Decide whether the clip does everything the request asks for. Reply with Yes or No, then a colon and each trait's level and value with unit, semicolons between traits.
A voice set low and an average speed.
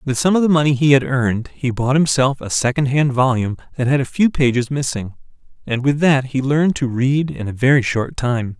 No: low, 130 Hz; fast, 225 wpm